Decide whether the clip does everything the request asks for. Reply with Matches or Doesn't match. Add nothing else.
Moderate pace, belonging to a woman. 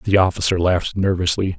Doesn't match